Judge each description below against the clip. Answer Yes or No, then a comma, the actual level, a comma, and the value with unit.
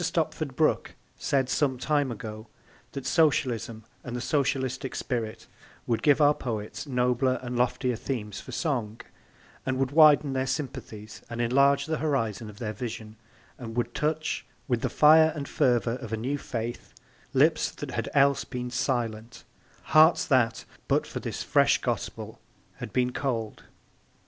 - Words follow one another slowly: No, average, 150 wpm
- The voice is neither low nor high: No, low, 125 Hz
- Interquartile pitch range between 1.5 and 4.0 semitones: Yes, average, 3.5 semitones